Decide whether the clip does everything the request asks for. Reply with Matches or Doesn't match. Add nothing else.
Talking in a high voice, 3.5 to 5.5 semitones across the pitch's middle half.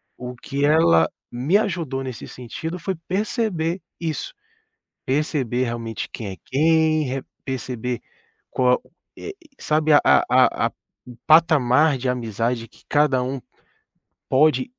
Doesn't match